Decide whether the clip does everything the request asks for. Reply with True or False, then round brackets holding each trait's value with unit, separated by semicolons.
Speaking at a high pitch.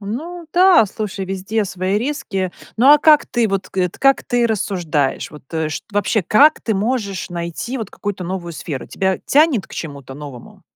True (200 Hz)